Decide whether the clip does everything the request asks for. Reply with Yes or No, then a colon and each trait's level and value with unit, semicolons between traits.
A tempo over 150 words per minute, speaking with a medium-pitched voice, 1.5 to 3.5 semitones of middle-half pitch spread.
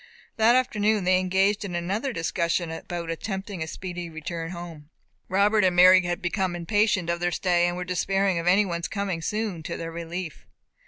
Yes: average, 180 wpm; medium, 180 Hz; narrow, 2.6 semitones